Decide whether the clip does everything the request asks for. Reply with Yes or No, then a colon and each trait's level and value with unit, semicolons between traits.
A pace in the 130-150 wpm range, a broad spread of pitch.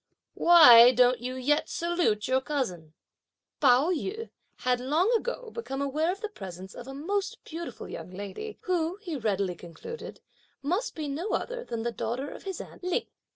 No: average, 170 wpm; wide, 7.2 semitones